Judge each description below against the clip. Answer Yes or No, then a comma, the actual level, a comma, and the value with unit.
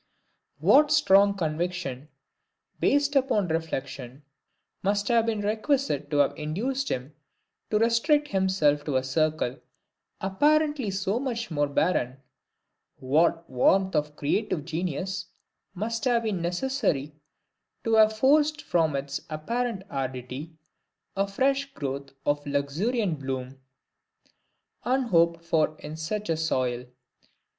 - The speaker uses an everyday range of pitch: No, wide, 7.8 semitones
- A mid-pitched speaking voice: Yes, medium, 180 Hz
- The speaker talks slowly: Yes, slow, 115 wpm